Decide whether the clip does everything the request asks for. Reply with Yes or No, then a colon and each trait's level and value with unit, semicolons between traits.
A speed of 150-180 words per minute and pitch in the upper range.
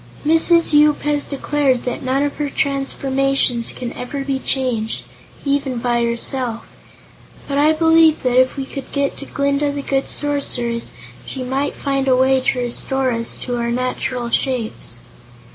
Yes: average, 160 wpm; very high, 270 Hz